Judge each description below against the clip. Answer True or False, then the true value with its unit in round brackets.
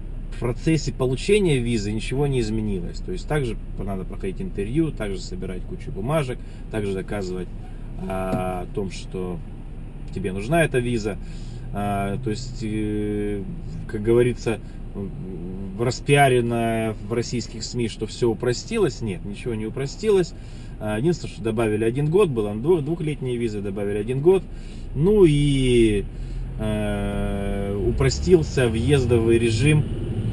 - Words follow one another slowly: False (125 wpm)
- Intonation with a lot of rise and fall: False (3.8 semitones)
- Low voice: True (115 Hz)